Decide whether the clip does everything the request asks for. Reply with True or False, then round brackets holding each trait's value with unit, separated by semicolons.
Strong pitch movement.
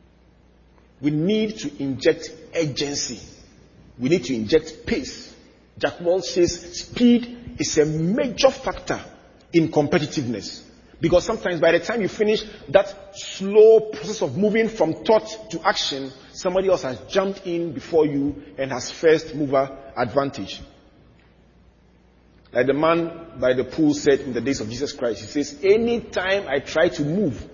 True (6.1 semitones)